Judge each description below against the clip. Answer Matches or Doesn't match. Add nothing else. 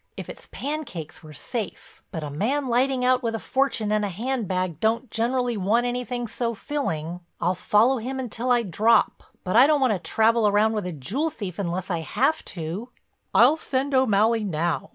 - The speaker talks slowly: Doesn't match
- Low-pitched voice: Doesn't match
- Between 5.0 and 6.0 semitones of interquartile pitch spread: Matches